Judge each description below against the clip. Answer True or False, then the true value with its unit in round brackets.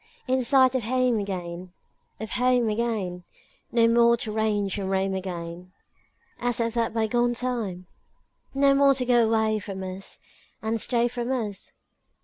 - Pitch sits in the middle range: False (225 Hz)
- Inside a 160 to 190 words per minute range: False (150 wpm)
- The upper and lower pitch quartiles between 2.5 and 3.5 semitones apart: False (3.9 semitones)